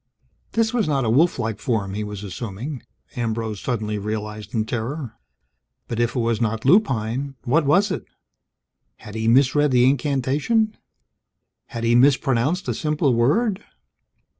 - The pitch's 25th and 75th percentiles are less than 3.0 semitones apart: No, average, 4.8 semitones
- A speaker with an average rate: Yes, average, 145 wpm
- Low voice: Yes, low, 120 Hz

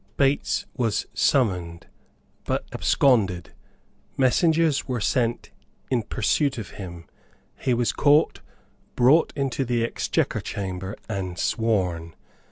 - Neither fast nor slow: No, slow, 105 wpm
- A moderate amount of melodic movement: No, wide, 6.2 semitones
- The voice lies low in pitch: Yes, low, 115 Hz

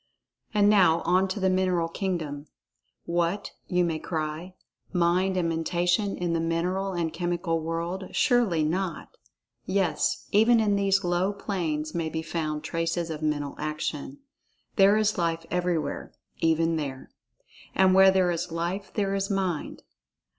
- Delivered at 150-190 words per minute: No, average, 140 wpm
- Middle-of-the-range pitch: Yes, medium, 175 Hz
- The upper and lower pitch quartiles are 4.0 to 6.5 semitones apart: No, average, 2.7 semitones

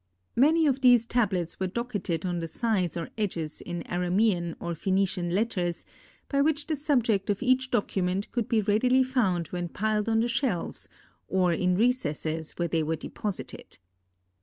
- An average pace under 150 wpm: No, average, 160 wpm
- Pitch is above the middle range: Yes, high, 200 Hz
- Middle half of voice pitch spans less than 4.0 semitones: No, wide, 5.6 semitones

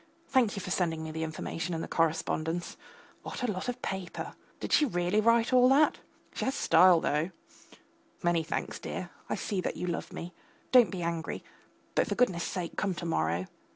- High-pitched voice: No, medium, 175 Hz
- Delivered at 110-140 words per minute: No, average, 190 wpm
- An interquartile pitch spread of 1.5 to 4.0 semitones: No, average, 4.8 semitones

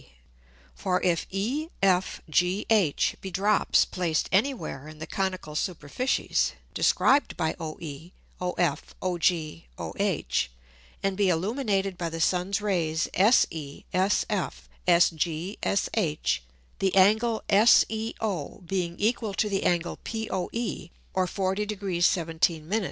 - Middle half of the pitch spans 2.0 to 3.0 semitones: No, average, 3.6 semitones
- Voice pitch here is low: No, medium, 185 Hz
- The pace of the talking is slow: Yes, slow, 120 wpm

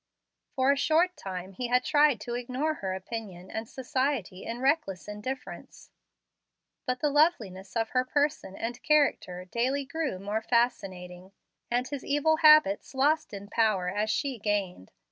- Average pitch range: No, wide, 6.3 semitones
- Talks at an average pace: Yes, average, 150 wpm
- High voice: Yes, high, 240 Hz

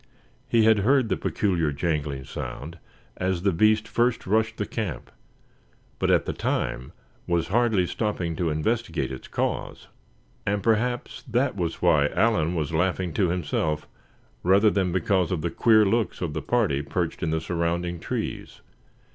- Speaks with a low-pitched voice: Yes, very low, 90 Hz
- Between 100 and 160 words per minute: Yes, average, 155 wpm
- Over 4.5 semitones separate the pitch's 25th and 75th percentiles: Yes, average, 4.9 semitones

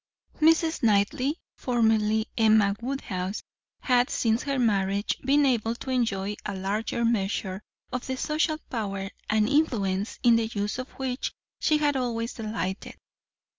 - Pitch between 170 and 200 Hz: No, high, 225 Hz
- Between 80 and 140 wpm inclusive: Yes, slow, 135 wpm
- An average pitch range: Yes, average, 4.0 semitones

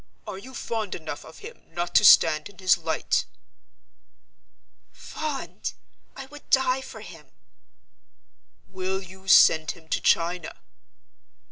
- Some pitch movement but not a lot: No, wide, 7.2 semitones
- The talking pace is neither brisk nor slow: No, slow, 125 wpm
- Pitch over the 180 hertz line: Yes, high, 190 Hz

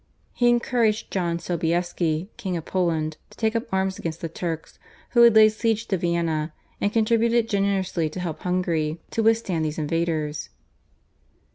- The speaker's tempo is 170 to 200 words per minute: No, average, 155 wpm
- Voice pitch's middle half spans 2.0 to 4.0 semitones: No, average, 5.0 semitones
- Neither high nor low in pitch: Yes, medium, 180 Hz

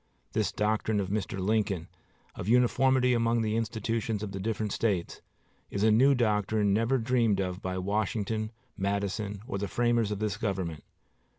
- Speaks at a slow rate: No, average, 160 wpm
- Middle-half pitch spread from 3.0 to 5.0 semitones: No, narrow, 2.5 semitones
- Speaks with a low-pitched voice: Yes, low, 105 Hz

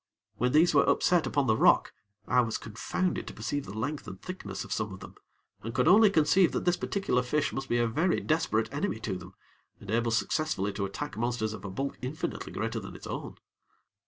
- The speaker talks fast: Yes, fast, 215 wpm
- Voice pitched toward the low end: Yes, low, 125 Hz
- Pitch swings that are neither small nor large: No, wide, 6.2 semitones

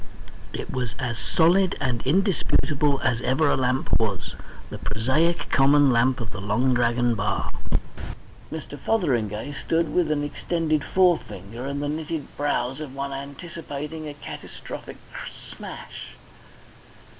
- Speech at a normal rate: No, slow, 130 wpm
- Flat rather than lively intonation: No, average, 4.2 semitones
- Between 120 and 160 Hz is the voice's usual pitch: Yes, medium, 140 Hz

